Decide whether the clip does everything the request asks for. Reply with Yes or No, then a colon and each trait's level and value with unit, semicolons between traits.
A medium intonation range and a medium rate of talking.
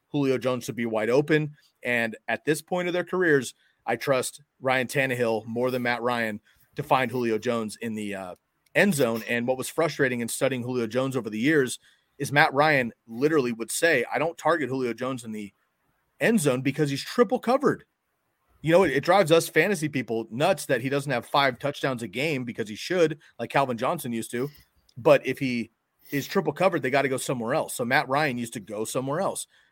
No: average, 3.9 semitones; fast, 210 wpm